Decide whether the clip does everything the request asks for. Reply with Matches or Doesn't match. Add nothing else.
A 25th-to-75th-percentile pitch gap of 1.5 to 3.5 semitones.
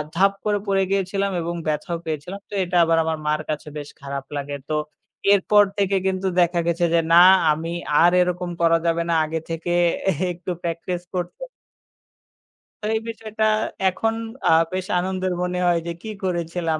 Matches